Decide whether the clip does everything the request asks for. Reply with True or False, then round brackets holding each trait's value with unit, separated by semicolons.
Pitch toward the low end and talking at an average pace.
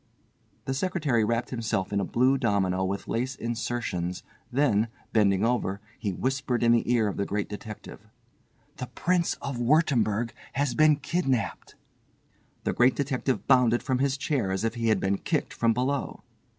True (120 Hz; 165 wpm)